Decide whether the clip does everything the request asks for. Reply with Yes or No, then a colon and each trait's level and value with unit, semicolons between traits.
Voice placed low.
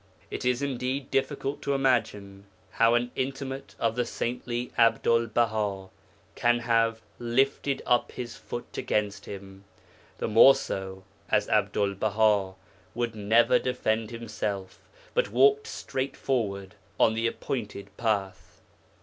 Yes: low, 115 Hz